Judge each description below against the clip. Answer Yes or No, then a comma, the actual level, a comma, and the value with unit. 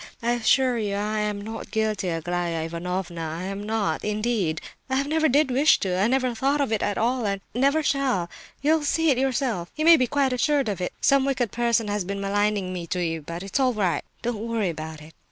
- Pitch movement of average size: No, wide, 6.2 semitones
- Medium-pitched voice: No, high, 215 Hz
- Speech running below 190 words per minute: No, fast, 205 wpm